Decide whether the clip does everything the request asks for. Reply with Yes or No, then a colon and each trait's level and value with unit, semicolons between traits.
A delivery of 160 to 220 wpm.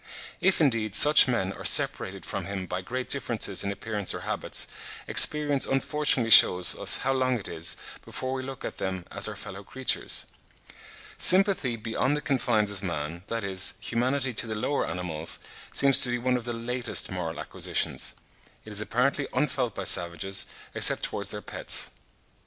Yes: average, 170 wpm